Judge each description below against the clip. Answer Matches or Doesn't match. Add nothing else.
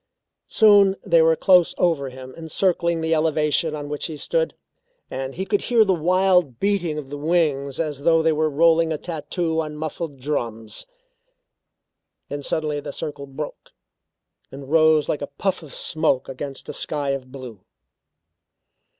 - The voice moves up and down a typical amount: Matches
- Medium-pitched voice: Matches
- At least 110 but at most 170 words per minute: Matches